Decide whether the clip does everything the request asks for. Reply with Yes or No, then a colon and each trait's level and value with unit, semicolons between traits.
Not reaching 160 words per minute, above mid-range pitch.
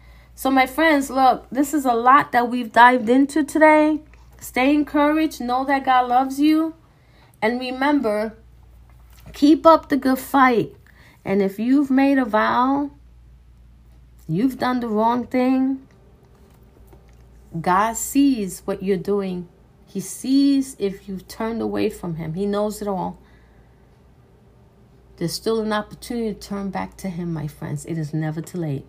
Yes: average, 145 wpm; high, 225 Hz